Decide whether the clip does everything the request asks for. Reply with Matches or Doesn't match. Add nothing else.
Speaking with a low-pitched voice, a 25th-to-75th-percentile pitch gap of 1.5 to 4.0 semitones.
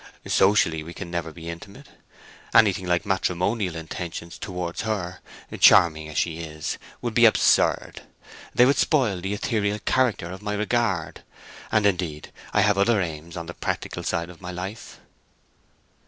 Matches